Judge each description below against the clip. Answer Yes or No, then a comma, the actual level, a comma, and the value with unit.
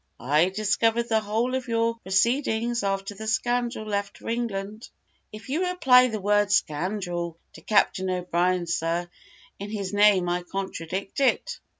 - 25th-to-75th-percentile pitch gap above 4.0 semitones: No, average, 3.7 semitones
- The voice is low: No, high, 205 Hz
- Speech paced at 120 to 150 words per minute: Yes, average, 145 wpm